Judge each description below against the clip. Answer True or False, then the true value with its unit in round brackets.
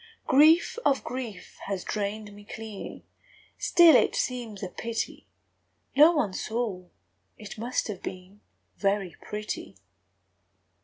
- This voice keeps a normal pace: False (115 wpm)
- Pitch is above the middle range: True (215 Hz)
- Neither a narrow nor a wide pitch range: True (4.0 semitones)